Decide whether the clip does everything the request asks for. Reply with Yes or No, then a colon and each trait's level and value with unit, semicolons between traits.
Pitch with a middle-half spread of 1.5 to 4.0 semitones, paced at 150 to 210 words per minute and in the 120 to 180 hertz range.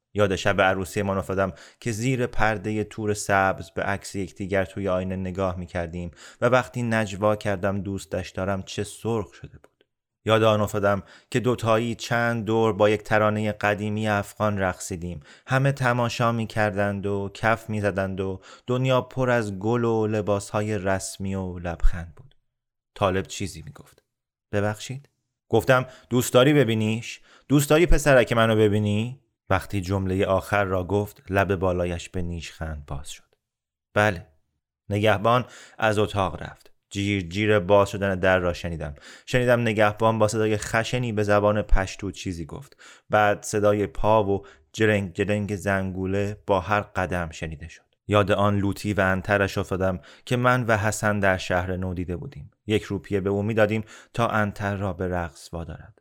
No: narrow, 2.6 semitones; fast, 155 wpm; low, 105 Hz